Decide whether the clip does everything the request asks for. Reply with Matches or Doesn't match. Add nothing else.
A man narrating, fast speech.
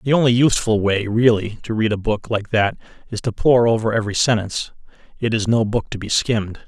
Matches